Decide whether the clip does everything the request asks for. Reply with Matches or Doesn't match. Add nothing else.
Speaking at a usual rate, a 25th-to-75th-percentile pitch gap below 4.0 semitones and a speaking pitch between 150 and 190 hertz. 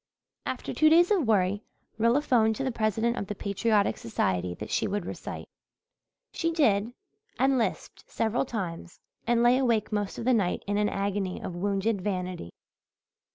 Doesn't match